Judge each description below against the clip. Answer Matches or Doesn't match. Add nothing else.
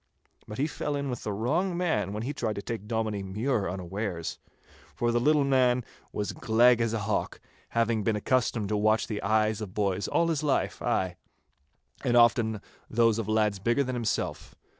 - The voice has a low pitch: Matches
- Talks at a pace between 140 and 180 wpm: Doesn't match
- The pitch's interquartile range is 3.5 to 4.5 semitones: Doesn't match